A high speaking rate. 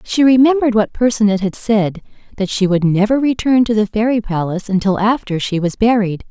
No: average, 190 wpm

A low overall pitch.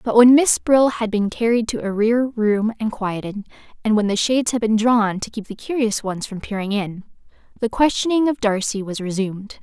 No: high, 220 Hz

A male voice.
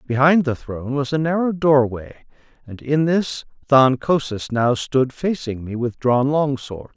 Yes: male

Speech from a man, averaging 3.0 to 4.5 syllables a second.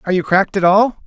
No: male; 7.4 syllables/s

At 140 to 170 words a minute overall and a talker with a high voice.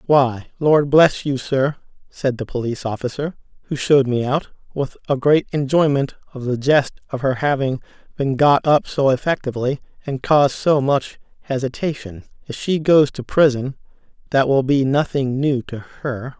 No: average, 165 wpm; low, 135 Hz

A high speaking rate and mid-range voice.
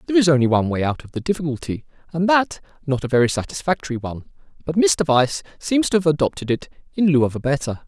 Yes: fast, 220 wpm; medium, 150 Hz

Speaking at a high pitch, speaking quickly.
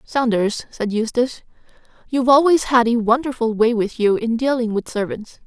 No: high, 235 Hz; average, 165 wpm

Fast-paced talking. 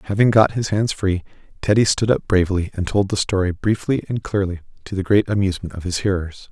Yes: fast, 210 wpm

